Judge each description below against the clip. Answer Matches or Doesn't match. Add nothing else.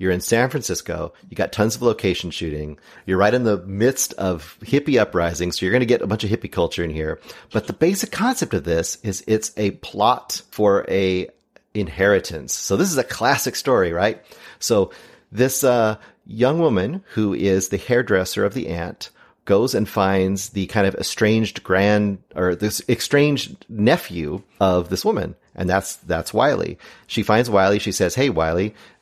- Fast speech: Doesn't match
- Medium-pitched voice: Doesn't match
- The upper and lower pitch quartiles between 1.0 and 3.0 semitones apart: Doesn't match